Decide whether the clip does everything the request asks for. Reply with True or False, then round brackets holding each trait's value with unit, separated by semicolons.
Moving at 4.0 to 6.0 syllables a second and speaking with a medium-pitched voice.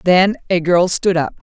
True (4.3 syllables/s; 180 Hz)